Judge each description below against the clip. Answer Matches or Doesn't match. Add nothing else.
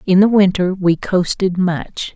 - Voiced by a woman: Matches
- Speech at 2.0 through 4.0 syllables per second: Matches